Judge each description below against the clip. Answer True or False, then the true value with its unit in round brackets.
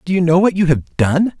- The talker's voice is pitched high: False (170 Hz)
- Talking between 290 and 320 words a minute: True (300 wpm)